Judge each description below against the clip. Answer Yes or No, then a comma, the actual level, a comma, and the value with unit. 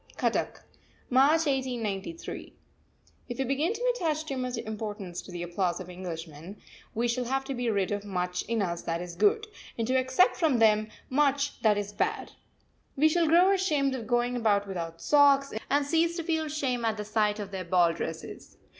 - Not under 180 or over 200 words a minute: Yes, average, 190 wpm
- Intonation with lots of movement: Yes, wide, 6.3 semitones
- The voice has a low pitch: No, high, 240 Hz